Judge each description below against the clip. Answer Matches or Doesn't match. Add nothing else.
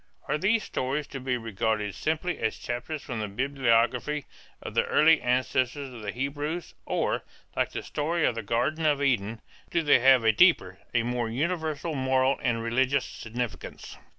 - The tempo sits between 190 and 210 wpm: Doesn't match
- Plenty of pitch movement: Doesn't match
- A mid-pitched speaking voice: Doesn't match